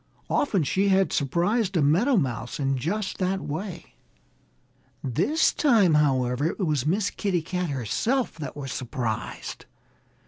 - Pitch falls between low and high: Yes, medium, 170 Hz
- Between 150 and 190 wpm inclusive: No, slow, 135 wpm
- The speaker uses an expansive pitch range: Yes, wide, 6.3 semitones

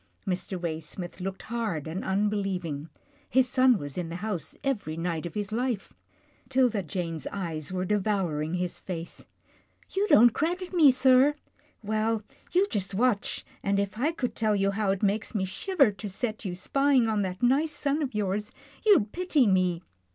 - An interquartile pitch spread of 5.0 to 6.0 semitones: Yes, wide, 5.6 semitones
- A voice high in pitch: Yes, high, 205 Hz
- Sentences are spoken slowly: No, average, 175 wpm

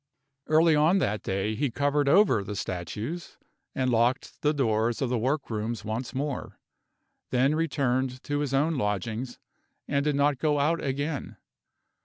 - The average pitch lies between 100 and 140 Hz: Yes, low, 135 Hz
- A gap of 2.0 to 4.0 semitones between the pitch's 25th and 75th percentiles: No, average, 4.4 semitones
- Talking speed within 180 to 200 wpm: No, average, 155 wpm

